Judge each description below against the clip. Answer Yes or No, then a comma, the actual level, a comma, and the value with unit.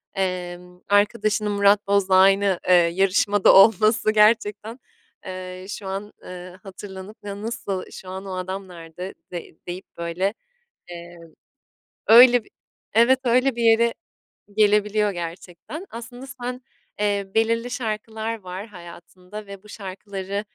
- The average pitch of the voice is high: Yes, high, 200 Hz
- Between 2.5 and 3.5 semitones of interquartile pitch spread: Yes, average, 2.9 semitones